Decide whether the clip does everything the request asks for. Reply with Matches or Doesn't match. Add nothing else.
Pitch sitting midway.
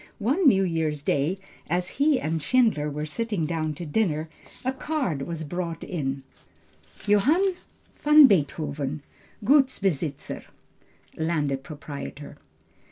Matches